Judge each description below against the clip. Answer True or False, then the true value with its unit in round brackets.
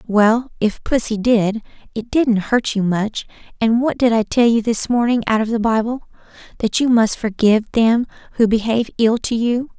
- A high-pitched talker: True (225 Hz)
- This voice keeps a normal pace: True (185 wpm)